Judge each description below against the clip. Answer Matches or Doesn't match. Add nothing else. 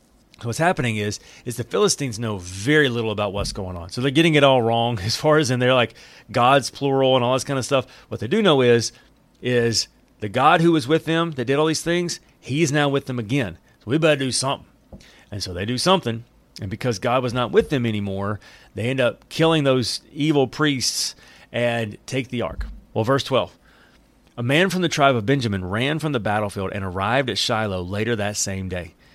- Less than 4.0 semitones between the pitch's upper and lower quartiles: Doesn't match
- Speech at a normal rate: Doesn't match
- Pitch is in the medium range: Doesn't match